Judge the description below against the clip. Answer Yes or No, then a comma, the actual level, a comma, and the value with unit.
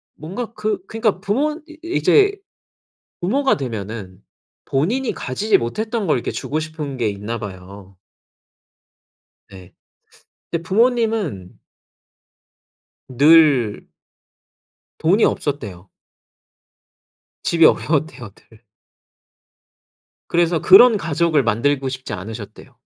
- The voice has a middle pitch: Yes, medium, 155 Hz